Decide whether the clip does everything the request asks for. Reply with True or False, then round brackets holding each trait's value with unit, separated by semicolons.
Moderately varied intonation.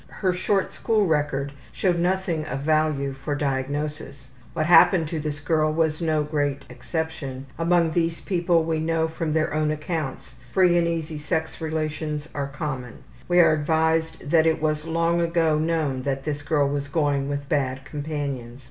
False (2.3 semitones)